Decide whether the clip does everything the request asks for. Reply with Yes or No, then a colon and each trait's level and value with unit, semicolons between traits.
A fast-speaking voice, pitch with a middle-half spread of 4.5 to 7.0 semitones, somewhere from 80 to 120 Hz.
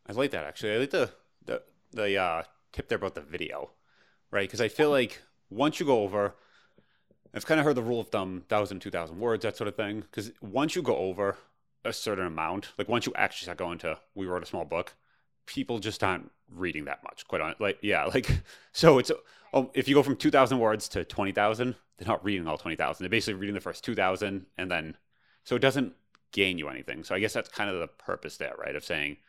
Yes: fast, 230 wpm; average, 5.0 semitones; low, 105 Hz